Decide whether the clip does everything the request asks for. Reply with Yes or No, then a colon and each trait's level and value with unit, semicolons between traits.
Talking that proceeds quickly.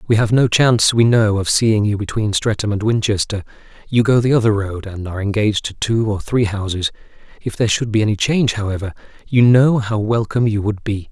Yes: fast, 215 wpm